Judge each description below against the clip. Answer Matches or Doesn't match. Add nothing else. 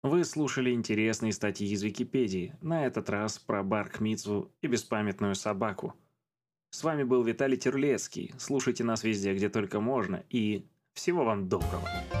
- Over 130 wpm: Matches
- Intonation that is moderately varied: Matches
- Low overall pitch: Matches